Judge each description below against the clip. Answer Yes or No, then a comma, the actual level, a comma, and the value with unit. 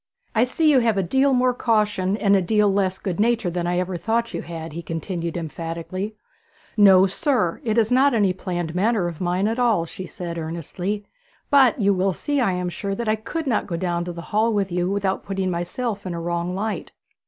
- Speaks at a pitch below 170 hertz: No, high, 195 Hz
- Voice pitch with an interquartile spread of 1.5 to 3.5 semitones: No, average, 4.1 semitones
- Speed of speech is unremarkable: No, fast, 220 wpm